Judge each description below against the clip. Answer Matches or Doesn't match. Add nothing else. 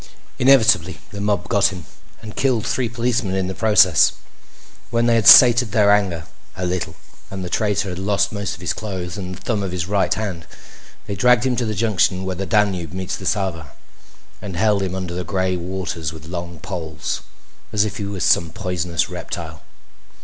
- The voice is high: Doesn't match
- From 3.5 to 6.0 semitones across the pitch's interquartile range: Doesn't match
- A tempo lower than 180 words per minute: Doesn't match